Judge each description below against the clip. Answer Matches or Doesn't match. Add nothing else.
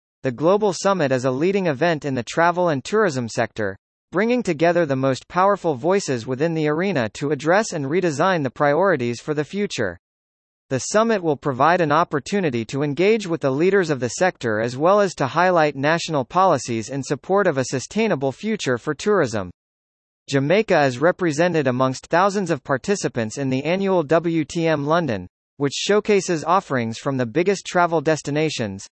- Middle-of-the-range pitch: Matches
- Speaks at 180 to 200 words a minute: Doesn't match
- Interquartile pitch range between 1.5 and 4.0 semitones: Doesn't match